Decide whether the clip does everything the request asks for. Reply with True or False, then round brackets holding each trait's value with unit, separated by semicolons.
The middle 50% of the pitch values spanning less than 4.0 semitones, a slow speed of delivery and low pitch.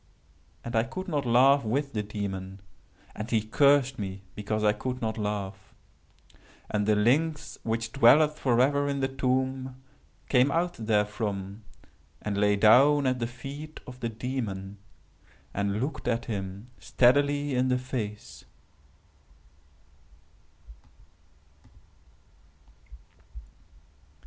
False (4.4 semitones; 115 wpm; 120 Hz)